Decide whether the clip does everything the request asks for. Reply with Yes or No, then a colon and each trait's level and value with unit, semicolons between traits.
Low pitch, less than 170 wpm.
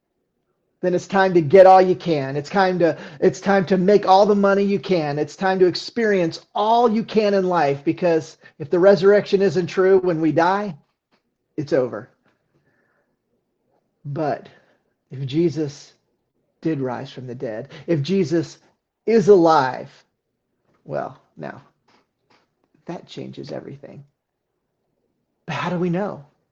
No: medium, 180 Hz; average, 140 wpm